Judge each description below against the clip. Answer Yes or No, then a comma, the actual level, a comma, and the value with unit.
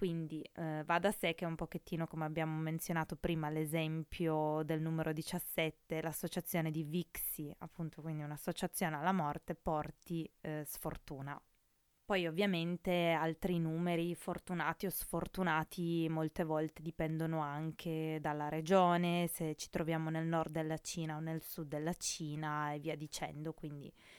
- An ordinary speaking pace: Yes, average, 140 wpm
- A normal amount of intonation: No, narrow, 1.7 semitones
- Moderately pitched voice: Yes, medium, 160 Hz